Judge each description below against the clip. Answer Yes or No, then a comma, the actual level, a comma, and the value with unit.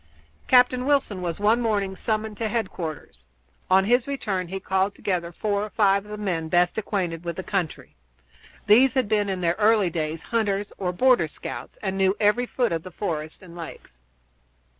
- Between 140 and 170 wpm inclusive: No, average, 180 wpm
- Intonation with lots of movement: No, average, 3.7 semitones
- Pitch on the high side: Yes, high, 195 Hz